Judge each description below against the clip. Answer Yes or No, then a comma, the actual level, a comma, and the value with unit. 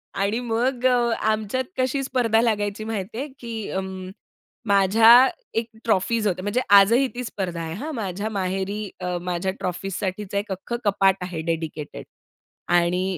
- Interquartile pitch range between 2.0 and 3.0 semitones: No, average, 3.5 semitones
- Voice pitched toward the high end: Yes, high, 205 Hz